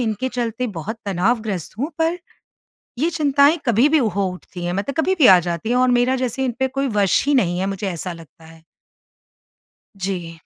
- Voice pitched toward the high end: Yes, high, 225 Hz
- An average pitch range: No, wide, 6.4 semitones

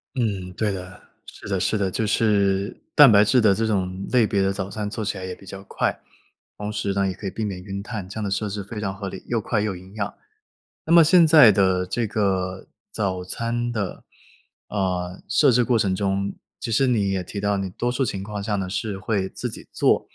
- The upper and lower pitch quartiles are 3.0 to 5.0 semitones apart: No, narrow, 2.4 semitones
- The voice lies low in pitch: Yes, low, 100 Hz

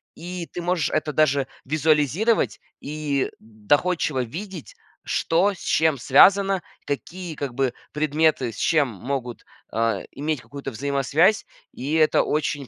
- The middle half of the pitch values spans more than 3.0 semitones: Yes, average, 3.6 semitones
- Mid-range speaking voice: Yes, medium, 150 Hz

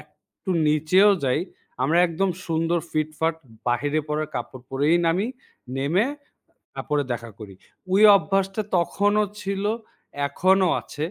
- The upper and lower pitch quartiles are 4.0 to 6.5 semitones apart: Yes, average, 4.5 semitones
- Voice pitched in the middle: Yes, medium, 165 Hz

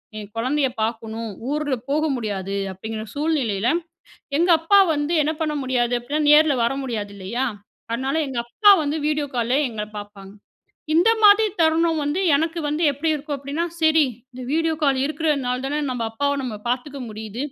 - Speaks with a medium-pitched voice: No, very high, 275 Hz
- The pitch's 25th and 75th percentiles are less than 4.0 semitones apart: No, average, 5.0 semitones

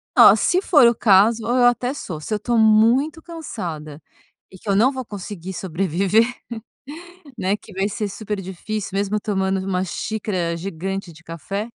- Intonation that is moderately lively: Yes, average, 3.3 semitones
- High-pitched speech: Yes, high, 200 Hz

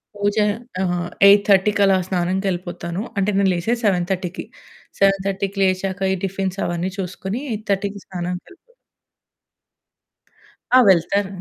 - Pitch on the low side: No, high, 190 Hz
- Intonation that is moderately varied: No, narrow, 1.7 semitones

